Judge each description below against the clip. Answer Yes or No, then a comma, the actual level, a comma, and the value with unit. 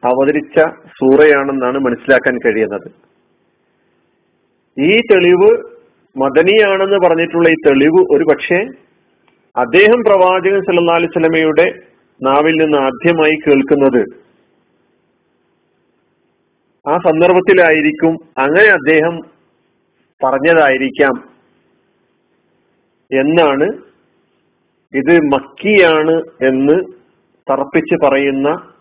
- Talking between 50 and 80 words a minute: Yes, average, 65 wpm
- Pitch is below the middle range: No, medium, 160 Hz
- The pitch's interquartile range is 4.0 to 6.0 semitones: Yes, average, 4.4 semitones